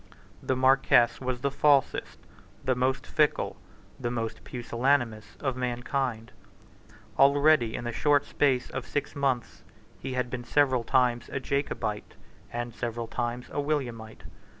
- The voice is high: No, low, 125 Hz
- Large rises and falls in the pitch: No, narrow, 2.6 semitones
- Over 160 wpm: No, slow, 135 wpm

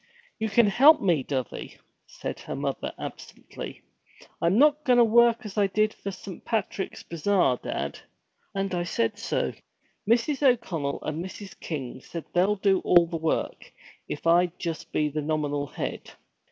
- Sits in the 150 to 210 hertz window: Yes, high, 190 Hz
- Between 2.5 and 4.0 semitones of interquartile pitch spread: No, wide, 5.5 semitones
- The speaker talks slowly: No, average, 160 wpm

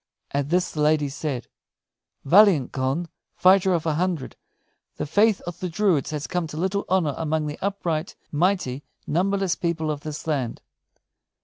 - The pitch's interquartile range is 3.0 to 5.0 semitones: Yes, average, 3.9 semitones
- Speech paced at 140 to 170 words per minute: Yes, average, 155 wpm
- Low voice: No, medium, 160 Hz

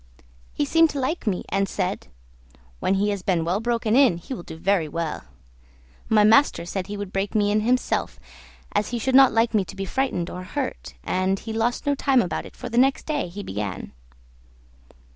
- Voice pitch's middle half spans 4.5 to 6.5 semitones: Yes, average, 5.2 semitones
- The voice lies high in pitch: Yes, high, 205 Hz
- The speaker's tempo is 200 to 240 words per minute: Yes, fast, 205 wpm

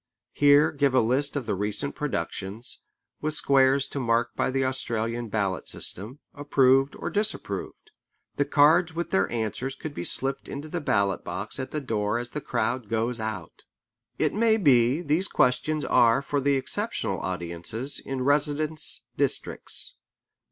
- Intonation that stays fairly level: No, average, 4.2 semitones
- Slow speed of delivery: No, average, 155 wpm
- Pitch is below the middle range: Yes, low, 130 Hz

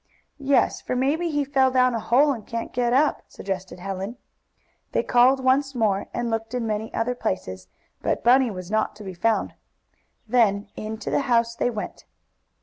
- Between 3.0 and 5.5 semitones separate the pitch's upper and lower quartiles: Yes, average, 3.5 semitones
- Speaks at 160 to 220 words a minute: Yes, average, 175 wpm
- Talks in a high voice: Yes, high, 235 Hz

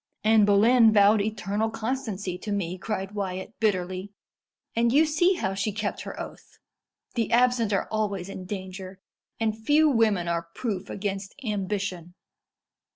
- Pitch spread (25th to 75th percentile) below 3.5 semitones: Yes, average, 2.8 semitones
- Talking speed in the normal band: Yes, average, 145 wpm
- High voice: Yes, high, 205 Hz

